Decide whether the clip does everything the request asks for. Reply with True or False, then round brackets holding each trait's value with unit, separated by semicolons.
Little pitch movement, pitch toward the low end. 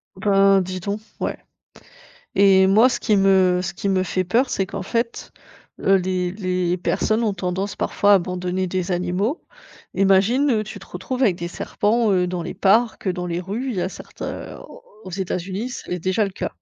False (2.2 semitones; 190 Hz)